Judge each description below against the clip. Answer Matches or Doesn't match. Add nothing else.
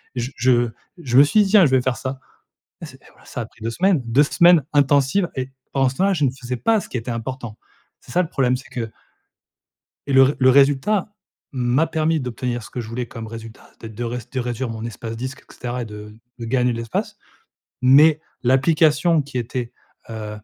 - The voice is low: Matches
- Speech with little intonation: Doesn't match